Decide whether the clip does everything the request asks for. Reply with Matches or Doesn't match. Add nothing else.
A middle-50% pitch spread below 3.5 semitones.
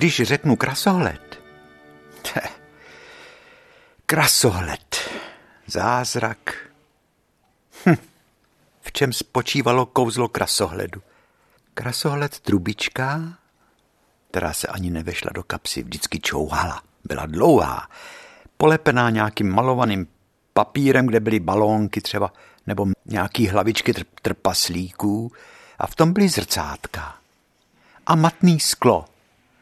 Doesn't match